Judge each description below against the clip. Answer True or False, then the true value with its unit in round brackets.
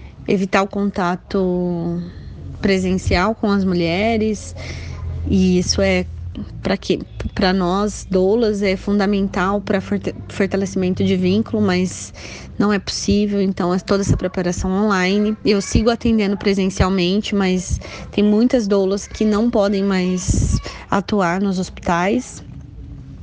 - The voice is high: True (195 Hz)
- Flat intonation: True (2.0 semitones)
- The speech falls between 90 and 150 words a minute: True (120 wpm)